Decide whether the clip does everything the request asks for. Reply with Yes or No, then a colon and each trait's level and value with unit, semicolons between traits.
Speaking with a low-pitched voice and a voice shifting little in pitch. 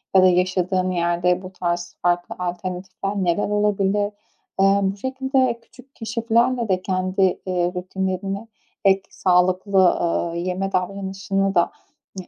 No: high, 190 Hz; narrow, 1.9 semitones